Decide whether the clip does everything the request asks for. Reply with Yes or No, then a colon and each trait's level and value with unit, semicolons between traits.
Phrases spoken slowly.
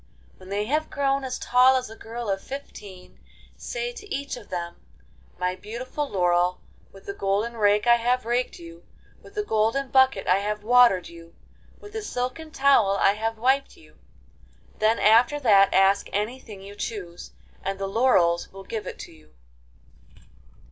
No: average, 170 wpm